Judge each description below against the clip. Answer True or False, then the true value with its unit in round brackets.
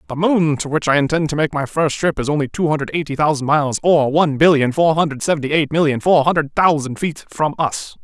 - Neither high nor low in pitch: True (150 Hz)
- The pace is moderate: False (240 wpm)